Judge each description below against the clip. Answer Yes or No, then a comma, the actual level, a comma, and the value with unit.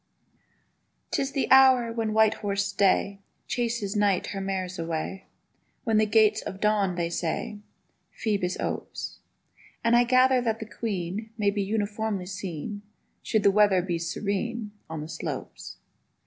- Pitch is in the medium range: No, high, 205 Hz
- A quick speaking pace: No, average, 145 wpm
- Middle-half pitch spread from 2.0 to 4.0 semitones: Yes, average, 2.7 semitones